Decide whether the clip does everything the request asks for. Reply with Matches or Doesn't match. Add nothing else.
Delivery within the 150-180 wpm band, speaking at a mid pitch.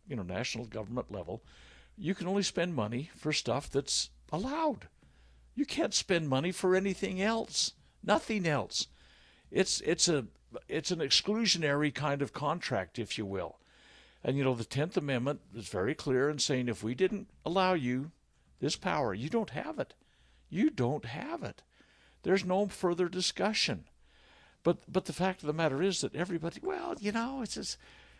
Matches